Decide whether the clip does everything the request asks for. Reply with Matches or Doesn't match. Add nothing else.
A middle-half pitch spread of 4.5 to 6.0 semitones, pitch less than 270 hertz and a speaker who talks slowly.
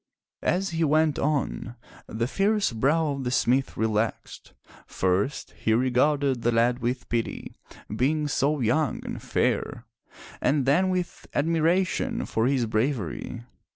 Matches